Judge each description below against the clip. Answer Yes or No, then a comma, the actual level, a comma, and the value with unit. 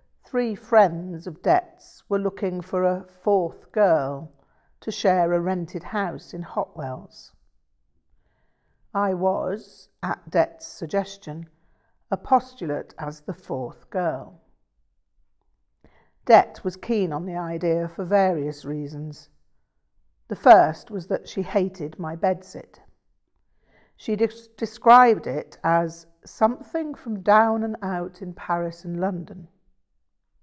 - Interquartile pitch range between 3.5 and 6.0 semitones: Yes, average, 4.1 semitones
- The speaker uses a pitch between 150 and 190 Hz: Yes, medium, 185 Hz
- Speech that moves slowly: Yes, slow, 115 wpm